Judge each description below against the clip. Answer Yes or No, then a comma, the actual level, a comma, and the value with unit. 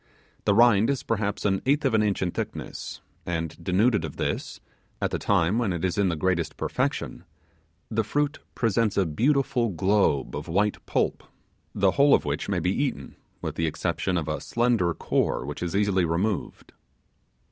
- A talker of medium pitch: No, low, 100 Hz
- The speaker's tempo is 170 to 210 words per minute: Yes, average, 180 wpm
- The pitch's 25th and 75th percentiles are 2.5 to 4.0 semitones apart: No, average, 4.9 semitones